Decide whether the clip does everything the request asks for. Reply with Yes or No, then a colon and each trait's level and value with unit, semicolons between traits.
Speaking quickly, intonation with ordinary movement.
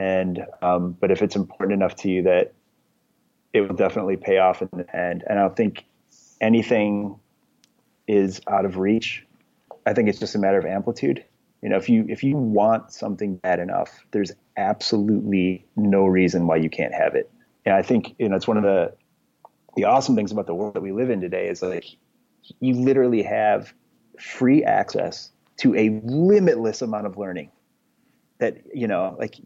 No: average, 185 wpm; average, 3.4 semitones